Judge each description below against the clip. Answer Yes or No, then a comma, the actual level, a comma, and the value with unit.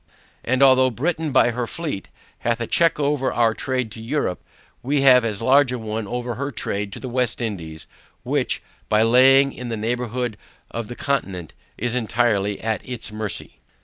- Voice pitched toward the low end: Yes, low, 120 Hz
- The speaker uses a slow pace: No, average, 180 wpm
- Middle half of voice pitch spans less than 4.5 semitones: Yes, average, 3.1 semitones